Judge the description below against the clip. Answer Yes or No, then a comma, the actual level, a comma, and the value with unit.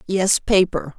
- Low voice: No, medium, 185 Hz